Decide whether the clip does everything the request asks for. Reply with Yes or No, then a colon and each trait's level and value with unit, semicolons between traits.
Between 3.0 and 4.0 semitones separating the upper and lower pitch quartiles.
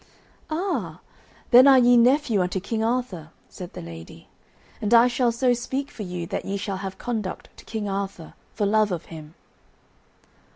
No: average, 4.7 semitones